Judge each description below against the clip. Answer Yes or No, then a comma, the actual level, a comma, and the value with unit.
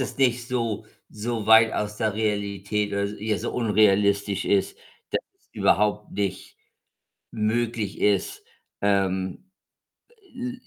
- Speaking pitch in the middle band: No, low, 105 Hz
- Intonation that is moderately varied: No, narrow, 2.0 semitones